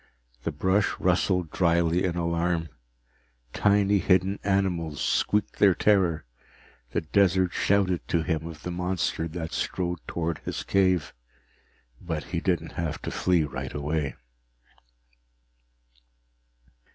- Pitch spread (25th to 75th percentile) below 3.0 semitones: Yes, narrow, 2.4 semitones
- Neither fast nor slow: No, slow, 115 wpm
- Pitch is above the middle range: No, very low, 85 Hz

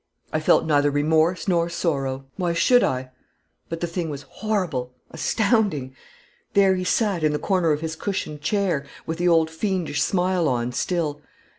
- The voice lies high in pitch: No, medium, 165 Hz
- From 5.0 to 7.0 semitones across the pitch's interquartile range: No, average, 4.0 semitones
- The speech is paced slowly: No, average, 165 wpm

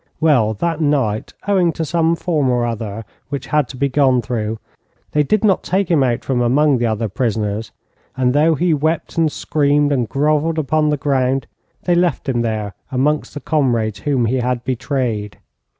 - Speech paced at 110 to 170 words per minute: No, average, 180 wpm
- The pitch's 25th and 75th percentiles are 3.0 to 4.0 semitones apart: No, average, 4.4 semitones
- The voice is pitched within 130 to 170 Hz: Yes, low, 135 Hz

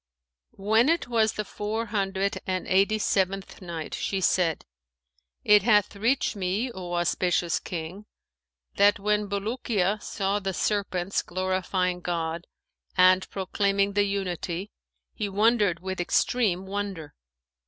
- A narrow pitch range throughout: Yes, narrow, 2.2 semitones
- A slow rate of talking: Yes, slow, 120 wpm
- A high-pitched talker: Yes, high, 195 Hz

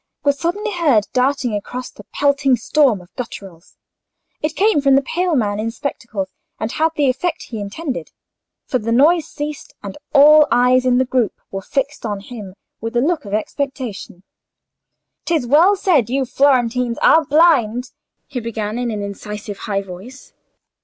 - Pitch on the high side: Yes, very high, 255 Hz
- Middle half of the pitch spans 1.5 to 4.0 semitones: No, average, 5.3 semitones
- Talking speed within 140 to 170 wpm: Yes, average, 165 wpm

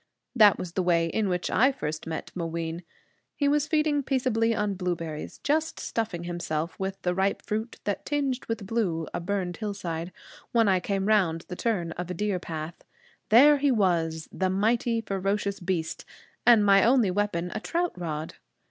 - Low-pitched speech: No, high, 195 Hz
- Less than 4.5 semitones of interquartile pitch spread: No, average, 4.8 semitones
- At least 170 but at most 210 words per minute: Yes, average, 175 wpm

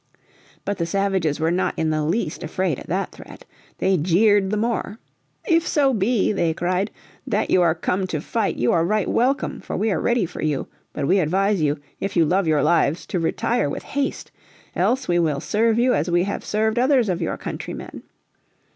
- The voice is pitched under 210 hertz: Yes, high, 190 Hz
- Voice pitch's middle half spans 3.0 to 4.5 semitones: No, average, 5.0 semitones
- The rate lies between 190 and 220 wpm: Yes, average, 200 wpm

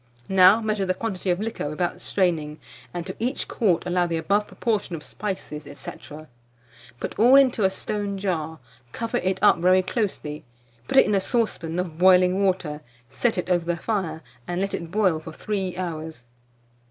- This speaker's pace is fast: No, average, 175 wpm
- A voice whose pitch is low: No, medium, 185 Hz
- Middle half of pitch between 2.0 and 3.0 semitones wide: No, average, 3.5 semitones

